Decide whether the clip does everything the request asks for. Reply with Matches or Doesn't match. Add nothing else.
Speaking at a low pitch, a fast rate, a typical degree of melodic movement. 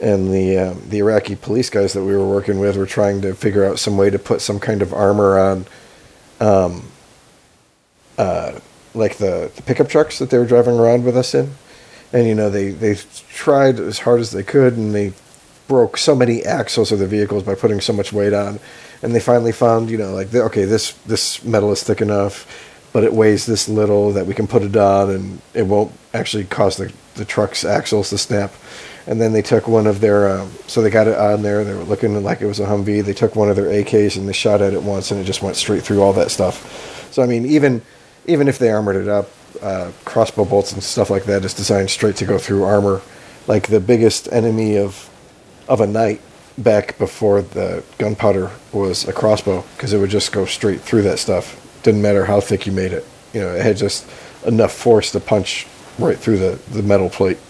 Doesn't match